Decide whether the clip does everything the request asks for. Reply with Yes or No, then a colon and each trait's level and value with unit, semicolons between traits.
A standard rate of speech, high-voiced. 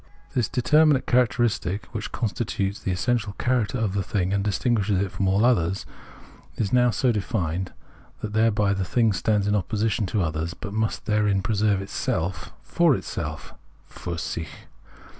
No: average, 155 wpm; low, 105 Hz